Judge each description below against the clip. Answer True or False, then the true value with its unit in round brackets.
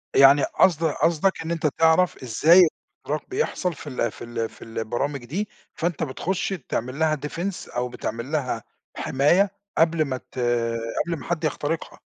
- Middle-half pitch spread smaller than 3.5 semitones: False (4.6 semitones)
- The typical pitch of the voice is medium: True (155 Hz)